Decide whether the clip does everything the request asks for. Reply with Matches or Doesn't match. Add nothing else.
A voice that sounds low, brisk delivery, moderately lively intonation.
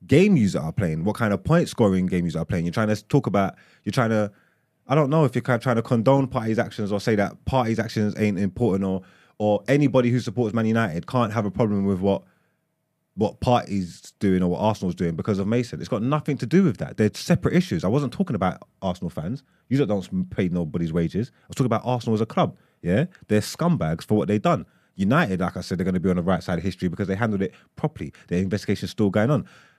Doesn't match